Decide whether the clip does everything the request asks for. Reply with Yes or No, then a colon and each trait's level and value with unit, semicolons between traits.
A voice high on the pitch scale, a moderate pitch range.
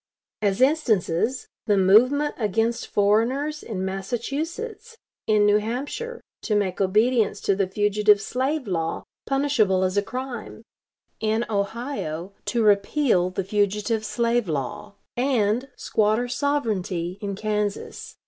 Yes: high, 215 Hz; average, 4.2 semitones